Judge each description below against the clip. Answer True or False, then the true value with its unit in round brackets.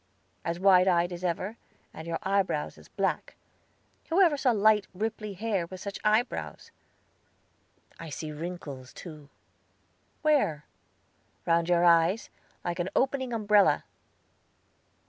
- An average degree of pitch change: True (4.3 semitones)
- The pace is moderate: False (125 wpm)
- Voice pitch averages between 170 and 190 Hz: True (185 Hz)